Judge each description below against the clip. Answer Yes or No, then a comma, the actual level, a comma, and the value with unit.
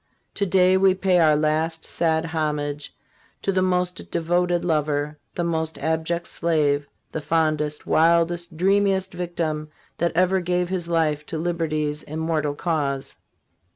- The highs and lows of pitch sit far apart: No, narrow, 2.5 semitones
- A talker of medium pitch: Yes, medium, 165 Hz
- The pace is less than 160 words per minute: Yes, slow, 135 wpm